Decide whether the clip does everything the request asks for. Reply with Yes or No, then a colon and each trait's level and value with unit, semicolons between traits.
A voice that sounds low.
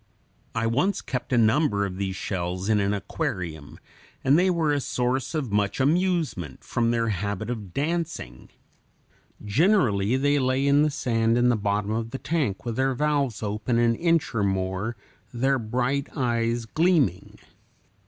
Yes: low, 120 Hz